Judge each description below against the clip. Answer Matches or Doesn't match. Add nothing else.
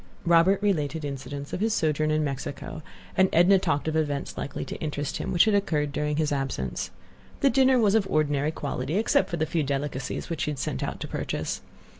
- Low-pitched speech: Doesn't match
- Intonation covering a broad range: Doesn't match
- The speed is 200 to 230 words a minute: Matches